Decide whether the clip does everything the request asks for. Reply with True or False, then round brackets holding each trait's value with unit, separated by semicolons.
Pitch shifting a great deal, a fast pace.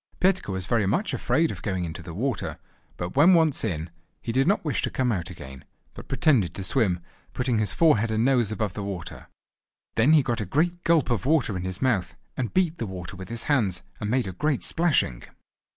True (7.4 semitones; 215 wpm)